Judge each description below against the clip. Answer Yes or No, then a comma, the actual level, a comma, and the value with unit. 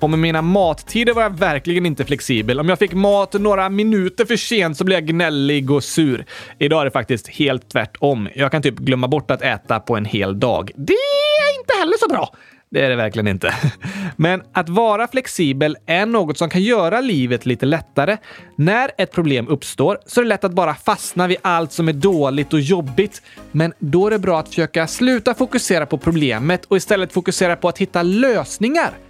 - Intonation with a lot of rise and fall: Yes, wide, 5.9 semitones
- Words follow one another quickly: Yes, fast, 205 wpm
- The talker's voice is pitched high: No, medium, 170 Hz